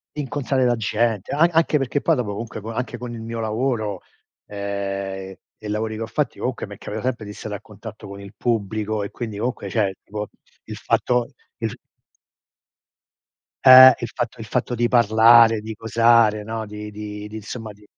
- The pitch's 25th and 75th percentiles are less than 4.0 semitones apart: Yes, narrow, 2.4 semitones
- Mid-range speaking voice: No, low, 110 Hz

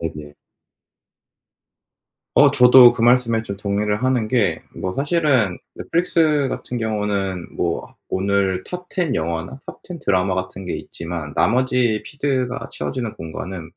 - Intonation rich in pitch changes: Yes, wide, 5.7 semitones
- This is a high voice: No, low, 110 Hz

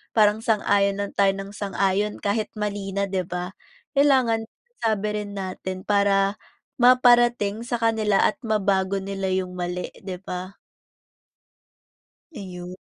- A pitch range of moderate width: No, narrow, 2.1 semitones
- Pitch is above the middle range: Yes, high, 200 Hz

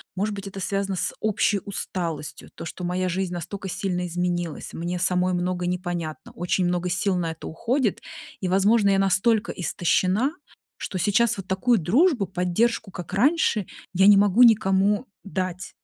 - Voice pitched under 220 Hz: Yes, high, 190 Hz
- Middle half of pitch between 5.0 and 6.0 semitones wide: No, narrow, 2.5 semitones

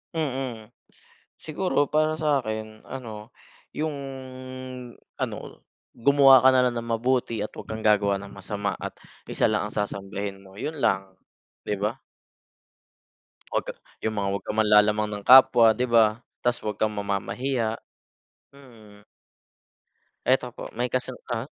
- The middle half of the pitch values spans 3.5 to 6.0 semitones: Yes, average, 3.9 semitones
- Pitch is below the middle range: Yes, low, 110 Hz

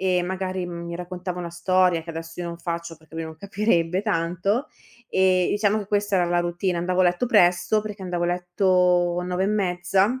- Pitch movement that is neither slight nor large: No, narrow, 1.7 semitones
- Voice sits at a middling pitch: Yes, medium, 180 Hz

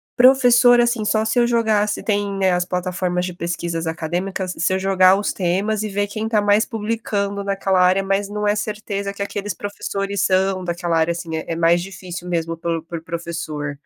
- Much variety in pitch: No, average, 3.1 semitones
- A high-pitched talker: Yes, high, 195 Hz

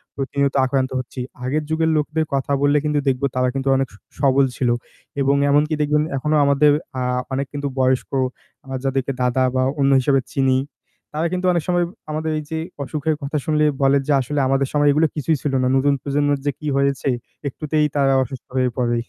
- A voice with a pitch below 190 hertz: Yes, medium, 140 Hz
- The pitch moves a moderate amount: No, narrow, 2.2 semitones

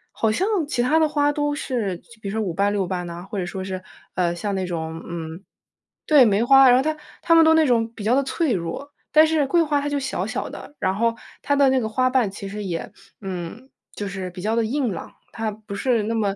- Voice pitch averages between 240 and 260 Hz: No, high, 220 Hz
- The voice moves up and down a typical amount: No, wide, 6.3 semitones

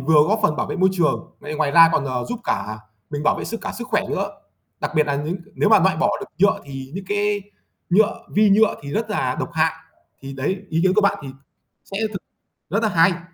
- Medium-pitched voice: Yes, medium, 180 Hz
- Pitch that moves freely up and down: Yes, wide, 5.7 semitones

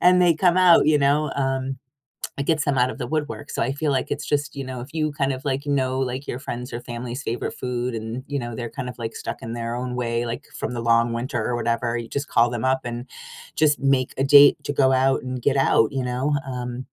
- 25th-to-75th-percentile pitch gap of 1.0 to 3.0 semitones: Yes, average, 2.7 semitones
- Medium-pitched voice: No, low, 130 Hz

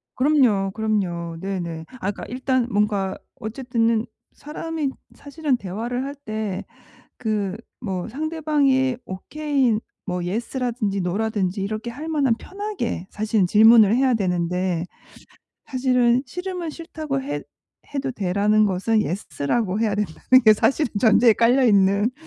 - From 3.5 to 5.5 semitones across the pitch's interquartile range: Yes, average, 5.1 semitones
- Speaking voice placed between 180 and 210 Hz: No, high, 225 Hz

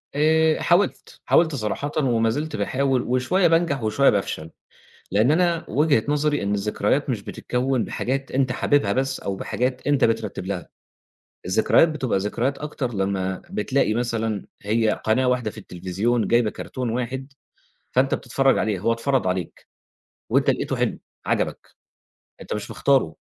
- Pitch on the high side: No, low, 125 Hz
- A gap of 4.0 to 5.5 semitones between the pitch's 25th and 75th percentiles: Yes, average, 4.7 semitones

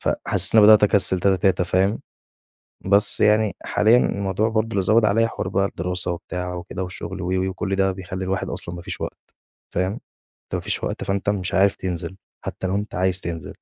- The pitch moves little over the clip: Yes, narrow, 1.9 semitones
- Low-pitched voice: Yes, very low, 95 Hz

